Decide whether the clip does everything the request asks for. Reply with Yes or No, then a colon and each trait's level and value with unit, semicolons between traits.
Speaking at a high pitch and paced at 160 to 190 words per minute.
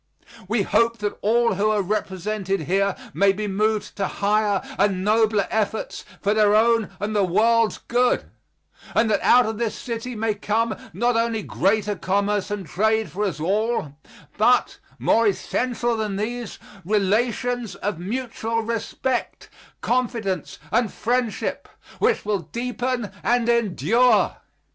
No: high, 215 Hz; average, 140 wpm